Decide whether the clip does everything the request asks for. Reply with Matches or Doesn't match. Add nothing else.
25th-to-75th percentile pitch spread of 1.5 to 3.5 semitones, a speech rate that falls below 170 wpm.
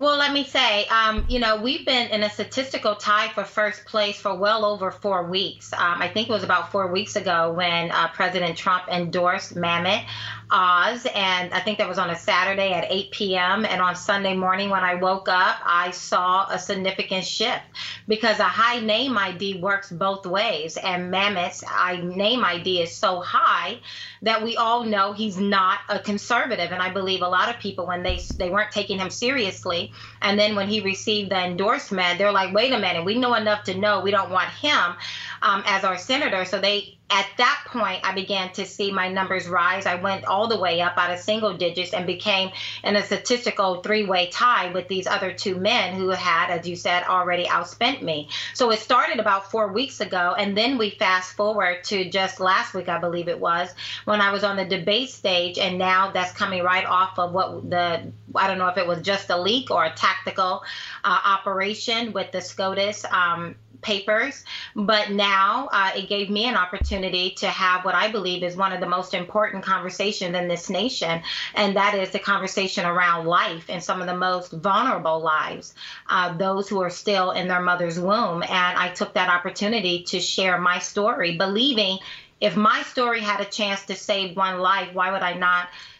Doesn't match